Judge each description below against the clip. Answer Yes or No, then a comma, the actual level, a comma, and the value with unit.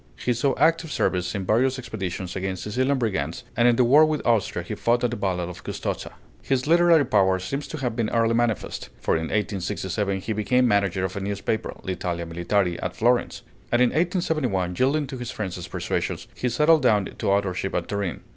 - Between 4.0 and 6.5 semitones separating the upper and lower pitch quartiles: Yes, average, 5.2 semitones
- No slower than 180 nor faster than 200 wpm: Yes, average, 195 wpm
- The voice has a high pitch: No, low, 110 Hz